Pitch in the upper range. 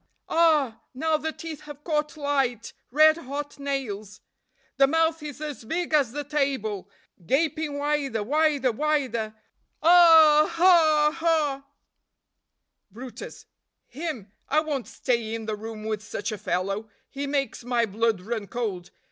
Yes: very high, 280 Hz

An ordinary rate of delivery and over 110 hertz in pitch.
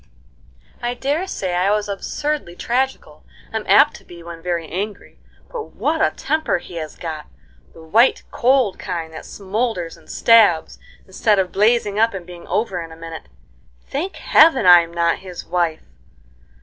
Yes: average, 160 wpm; high, 190 Hz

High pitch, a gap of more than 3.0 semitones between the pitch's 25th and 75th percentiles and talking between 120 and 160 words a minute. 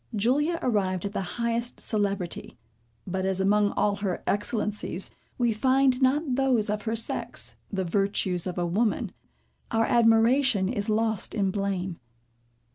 Yes: high, 210 Hz; average, 3.5 semitones; average, 140 wpm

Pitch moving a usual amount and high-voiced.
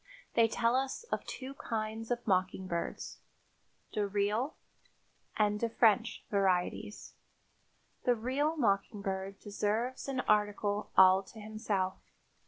Yes: average, 3.1 semitones; high, 210 Hz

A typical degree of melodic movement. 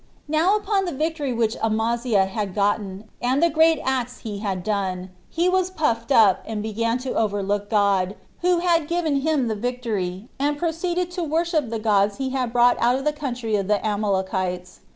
No: wide, 7.1 semitones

